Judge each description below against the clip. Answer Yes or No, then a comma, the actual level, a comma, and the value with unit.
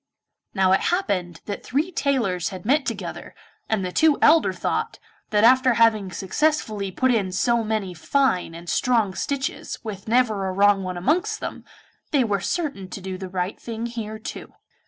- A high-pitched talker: Yes, high, 215 Hz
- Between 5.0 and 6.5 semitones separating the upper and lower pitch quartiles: Yes, wide, 5.4 semitones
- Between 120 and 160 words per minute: No, average, 175 wpm